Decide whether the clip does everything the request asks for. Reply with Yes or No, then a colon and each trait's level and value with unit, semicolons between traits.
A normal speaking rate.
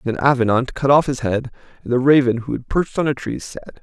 No: fast, 250 wpm